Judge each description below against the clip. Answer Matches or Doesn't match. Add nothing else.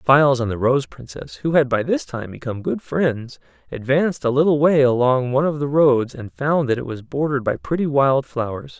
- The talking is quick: Matches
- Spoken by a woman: Doesn't match